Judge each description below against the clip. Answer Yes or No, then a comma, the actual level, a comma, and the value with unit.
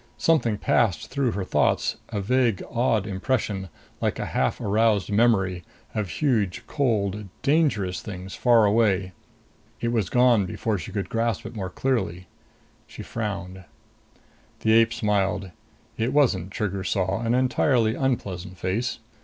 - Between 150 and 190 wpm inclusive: No, slow, 135 wpm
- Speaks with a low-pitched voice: Yes, low, 105 Hz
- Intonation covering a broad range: No, average, 3.7 semitones